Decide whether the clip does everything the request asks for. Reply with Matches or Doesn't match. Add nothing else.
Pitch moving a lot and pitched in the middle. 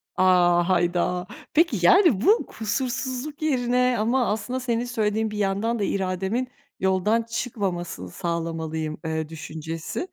Doesn't match